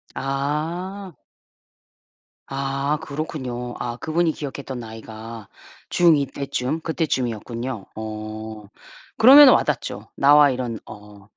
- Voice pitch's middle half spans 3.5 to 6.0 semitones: Yes, average, 5.2 semitones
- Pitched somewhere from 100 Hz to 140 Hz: Yes, low, 135 Hz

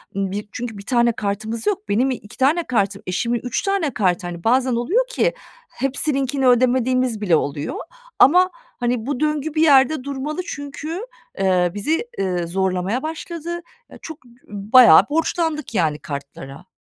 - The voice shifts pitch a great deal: Yes, wide, 7.3 semitones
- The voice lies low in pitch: No, very high, 250 Hz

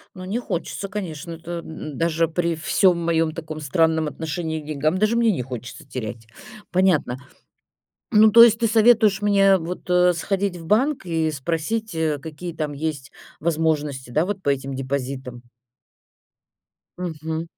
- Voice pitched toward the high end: No, medium, 165 Hz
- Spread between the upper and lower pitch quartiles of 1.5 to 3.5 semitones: No, average, 3.9 semitones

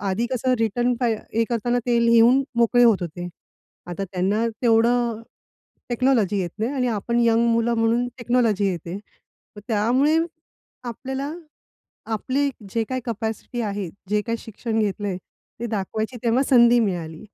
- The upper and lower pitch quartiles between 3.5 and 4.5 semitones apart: No, average, 2.7 semitones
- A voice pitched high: Yes, high, 230 Hz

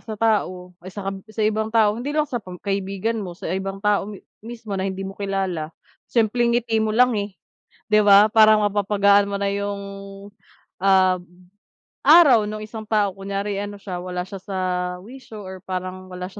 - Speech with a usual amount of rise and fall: No, narrow, 2.1 semitones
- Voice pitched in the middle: No, high, 200 Hz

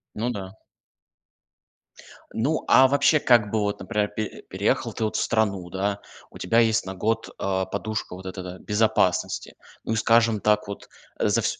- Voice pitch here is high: No, low, 105 Hz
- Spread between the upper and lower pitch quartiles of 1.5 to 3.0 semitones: Yes, average, 2.7 semitones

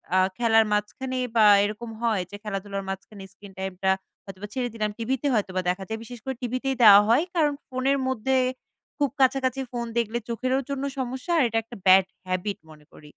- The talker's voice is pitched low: No, high, 225 Hz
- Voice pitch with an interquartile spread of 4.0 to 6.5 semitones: Yes, average, 4.4 semitones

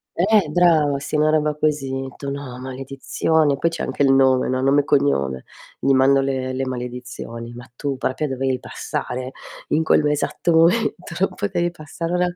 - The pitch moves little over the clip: No, average, 3.0 semitones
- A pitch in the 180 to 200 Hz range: No, medium, 140 Hz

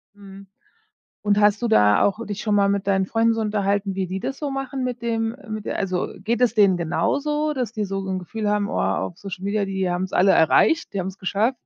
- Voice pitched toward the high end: Yes, high, 205 Hz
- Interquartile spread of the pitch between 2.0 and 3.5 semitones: Yes, average, 2.9 semitones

